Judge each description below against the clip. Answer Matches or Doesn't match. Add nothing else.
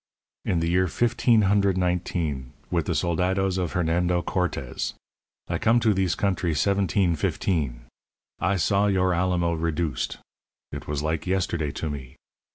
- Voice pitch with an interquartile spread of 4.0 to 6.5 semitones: Doesn't match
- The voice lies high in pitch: Doesn't match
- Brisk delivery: Doesn't match